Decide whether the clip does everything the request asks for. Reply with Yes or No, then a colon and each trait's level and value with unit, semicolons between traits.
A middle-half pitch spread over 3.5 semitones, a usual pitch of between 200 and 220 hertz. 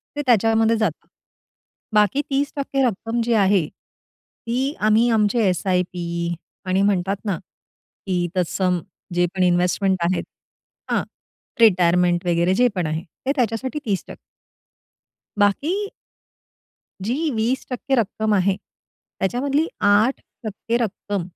Yes: average, 4.5 semitones; high, 205 Hz